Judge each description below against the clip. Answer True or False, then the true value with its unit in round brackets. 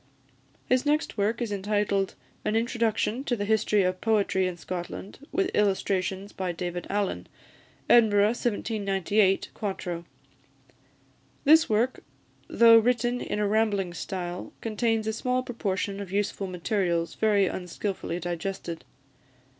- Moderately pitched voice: False (205 Hz)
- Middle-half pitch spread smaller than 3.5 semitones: True (3.1 semitones)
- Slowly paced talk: True (120 wpm)